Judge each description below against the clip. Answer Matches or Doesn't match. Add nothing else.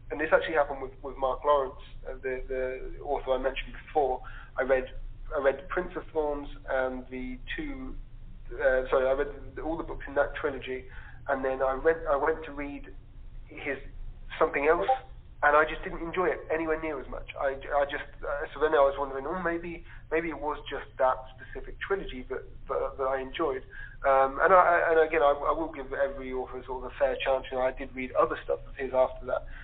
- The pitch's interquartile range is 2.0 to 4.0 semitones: Matches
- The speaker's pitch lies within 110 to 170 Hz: Matches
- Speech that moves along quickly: Matches